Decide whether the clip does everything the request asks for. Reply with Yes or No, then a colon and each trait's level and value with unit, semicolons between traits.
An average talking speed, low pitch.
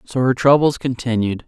Yes: average, 165 wpm; low, 125 Hz